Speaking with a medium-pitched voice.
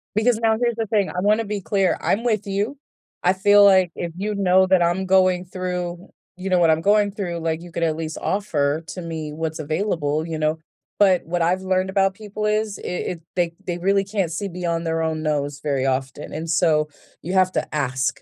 Yes: medium, 180 Hz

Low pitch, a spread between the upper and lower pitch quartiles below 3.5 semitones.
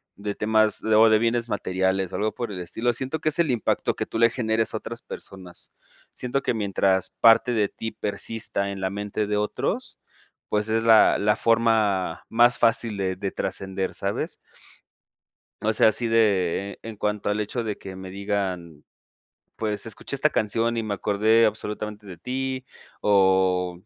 Yes: low, 105 Hz; average, 2.7 semitones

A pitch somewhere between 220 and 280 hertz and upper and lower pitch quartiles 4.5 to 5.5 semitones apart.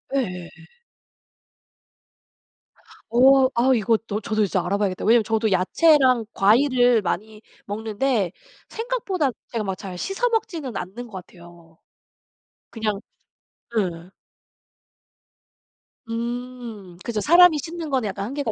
Yes: high, 225 Hz; average, 5.1 semitones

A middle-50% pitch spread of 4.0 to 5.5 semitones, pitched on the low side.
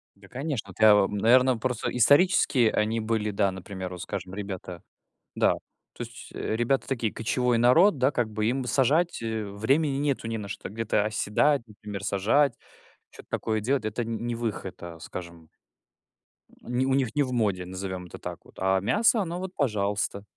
Yes: average, 4.6 semitones; low, 110 Hz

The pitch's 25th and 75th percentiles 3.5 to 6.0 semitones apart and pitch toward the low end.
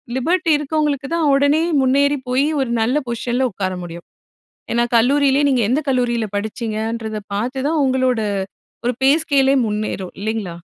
No: average, 4.0 semitones; very high, 255 Hz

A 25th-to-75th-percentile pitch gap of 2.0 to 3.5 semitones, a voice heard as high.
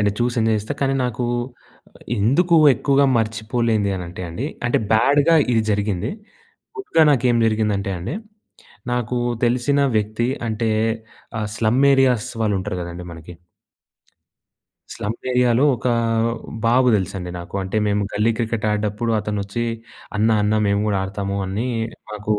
No: average, 3.2 semitones; low, 110 Hz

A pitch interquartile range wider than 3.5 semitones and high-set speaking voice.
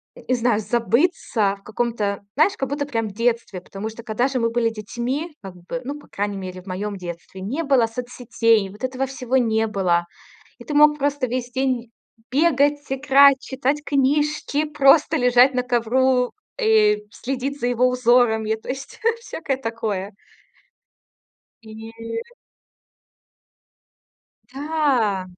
Yes: average, 4.0 semitones; high, 245 Hz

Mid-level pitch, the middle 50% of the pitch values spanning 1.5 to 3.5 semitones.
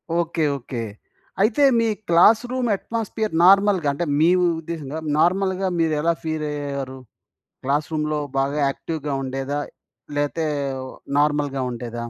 No: medium, 155 Hz; average, 4.5 semitones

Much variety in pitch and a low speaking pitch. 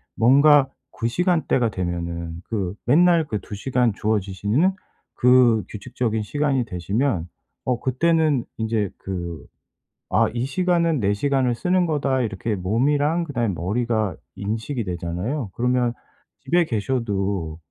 Yes: wide, 5.9 semitones; low, 120 Hz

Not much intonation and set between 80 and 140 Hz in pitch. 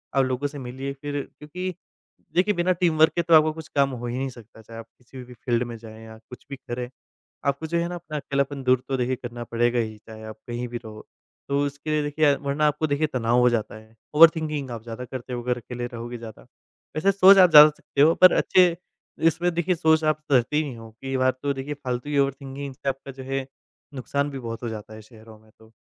No: average, 4.1 semitones; low, 135 Hz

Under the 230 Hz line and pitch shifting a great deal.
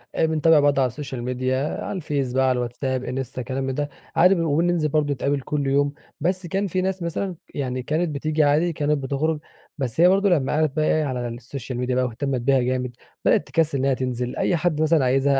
No: medium, 140 Hz; average, 3.4 semitones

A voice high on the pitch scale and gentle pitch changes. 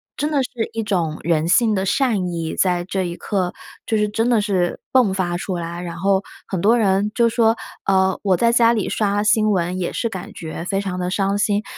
No: high, 195 Hz; average, 3.6 semitones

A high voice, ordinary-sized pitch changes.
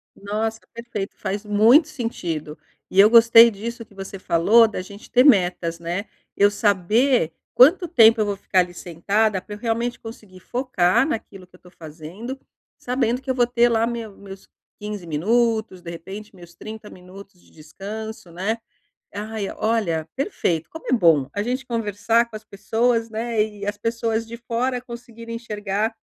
Yes: high, 215 Hz; average, 3.4 semitones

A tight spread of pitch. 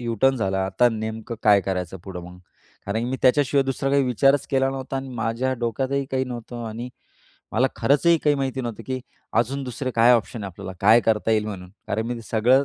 No: average, 3.3 semitones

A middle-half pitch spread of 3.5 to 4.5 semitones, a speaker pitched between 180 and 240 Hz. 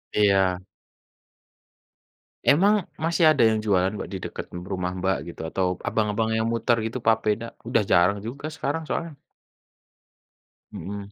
No: average, 4.0 semitones; low, 105 Hz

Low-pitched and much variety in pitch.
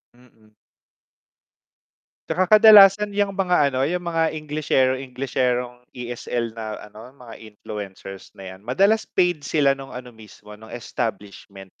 Yes: low, 125 Hz; wide, 6.7 semitones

